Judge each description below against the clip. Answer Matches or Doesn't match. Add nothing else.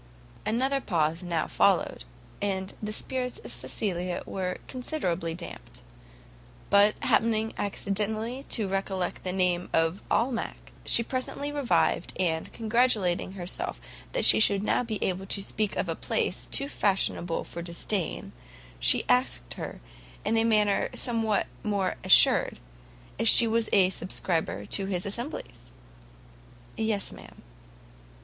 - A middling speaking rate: Doesn't match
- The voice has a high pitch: Matches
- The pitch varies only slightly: Doesn't match